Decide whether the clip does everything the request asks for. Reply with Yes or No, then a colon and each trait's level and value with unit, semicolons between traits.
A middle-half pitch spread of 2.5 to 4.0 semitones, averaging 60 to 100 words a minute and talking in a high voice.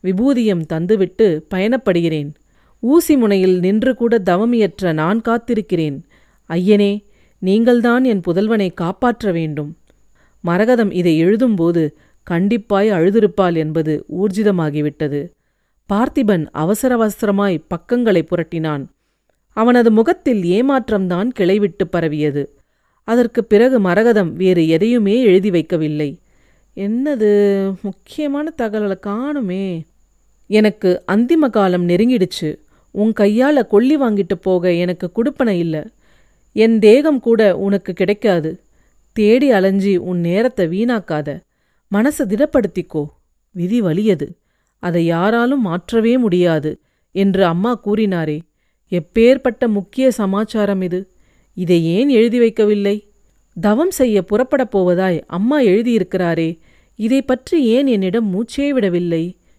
No: average, 4.8 semitones; average, 95 wpm; high, 200 Hz